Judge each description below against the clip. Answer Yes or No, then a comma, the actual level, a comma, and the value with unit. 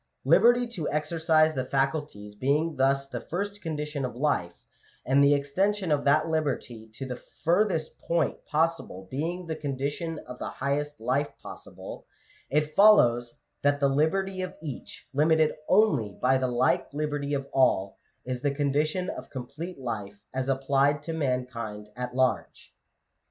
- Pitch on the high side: No, medium, 145 Hz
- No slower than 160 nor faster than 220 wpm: No, average, 150 wpm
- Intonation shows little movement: No, average, 3.6 semitones